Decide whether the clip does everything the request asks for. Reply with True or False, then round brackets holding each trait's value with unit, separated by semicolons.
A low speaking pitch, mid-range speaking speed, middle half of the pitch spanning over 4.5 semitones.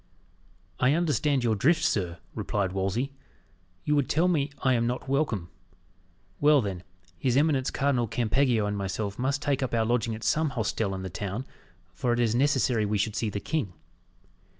True (120 Hz; 175 wpm; 5.2 semitones)